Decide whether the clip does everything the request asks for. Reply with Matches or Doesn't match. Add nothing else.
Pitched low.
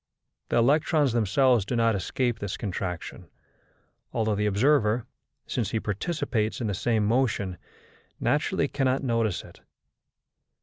Matches